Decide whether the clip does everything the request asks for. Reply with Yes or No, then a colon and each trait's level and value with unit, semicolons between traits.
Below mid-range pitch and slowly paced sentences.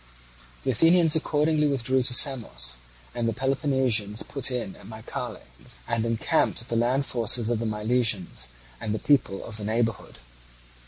No: low, 120 Hz; average, 155 wpm